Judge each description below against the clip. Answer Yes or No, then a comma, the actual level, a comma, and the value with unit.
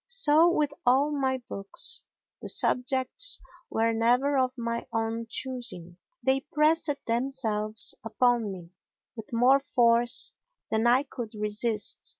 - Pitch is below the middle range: No, high, 245 Hz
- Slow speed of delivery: Yes, slow, 120 wpm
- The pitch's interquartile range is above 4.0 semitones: No, average, 3.3 semitones